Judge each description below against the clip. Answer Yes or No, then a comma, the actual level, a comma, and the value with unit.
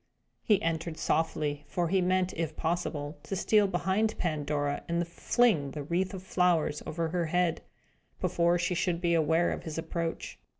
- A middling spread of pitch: No, narrow, 2.1 semitones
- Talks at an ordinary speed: Yes, average, 165 wpm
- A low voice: No, medium, 170 Hz